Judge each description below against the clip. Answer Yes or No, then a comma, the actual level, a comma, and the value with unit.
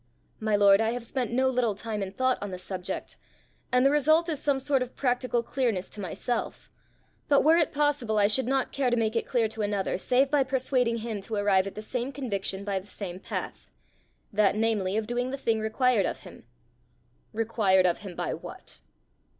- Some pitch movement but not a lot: Yes, average, 4.1 semitones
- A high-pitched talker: Yes, high, 230 Hz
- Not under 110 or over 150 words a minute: No, fast, 205 wpm